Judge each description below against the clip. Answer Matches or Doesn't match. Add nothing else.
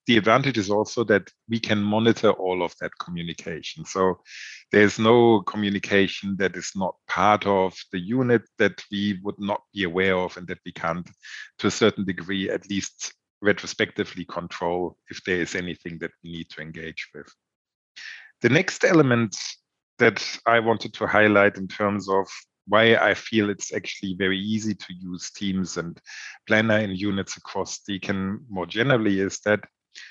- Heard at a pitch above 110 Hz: Doesn't match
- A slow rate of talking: Doesn't match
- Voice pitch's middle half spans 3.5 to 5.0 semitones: Doesn't match